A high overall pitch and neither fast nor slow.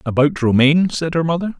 No: medium, 155 Hz; average, 190 wpm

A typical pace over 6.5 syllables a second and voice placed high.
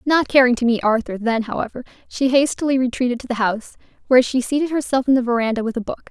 Yes: 6.9 syllables/s; very high, 250 Hz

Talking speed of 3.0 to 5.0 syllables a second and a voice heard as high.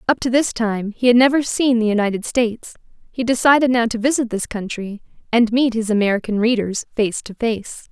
No: 5.4 syllables/s; high, 230 Hz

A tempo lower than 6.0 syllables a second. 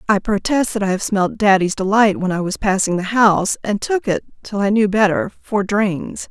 Yes: 5.0 syllables/s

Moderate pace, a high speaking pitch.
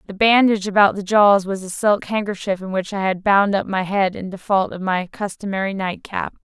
No: fast, 215 wpm; high, 195 Hz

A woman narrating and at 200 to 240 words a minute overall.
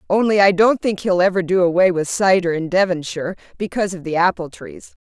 Yes: female; fast, 205 wpm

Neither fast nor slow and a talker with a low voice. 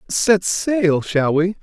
No: average, 150 wpm; medium, 185 Hz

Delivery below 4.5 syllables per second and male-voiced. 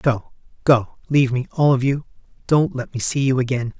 No: 5.2 syllables/s; male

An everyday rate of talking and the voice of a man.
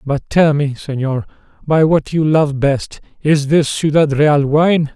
Yes: average, 170 wpm; male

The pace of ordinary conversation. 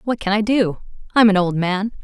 No: fast, 235 wpm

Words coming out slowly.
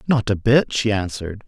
No: fast, 205 wpm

